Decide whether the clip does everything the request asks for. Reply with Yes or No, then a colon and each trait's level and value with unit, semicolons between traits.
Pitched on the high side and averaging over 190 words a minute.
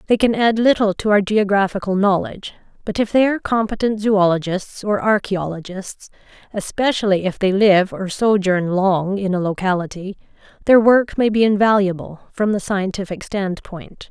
No: high, 200 Hz; average, 150 wpm